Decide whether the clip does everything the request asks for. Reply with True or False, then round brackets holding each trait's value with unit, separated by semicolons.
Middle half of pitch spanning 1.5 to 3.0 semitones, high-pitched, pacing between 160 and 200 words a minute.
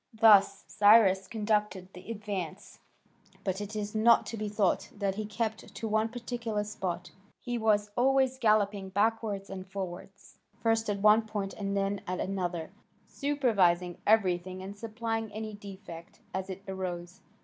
False (2.6 semitones; 205 Hz; 150 wpm)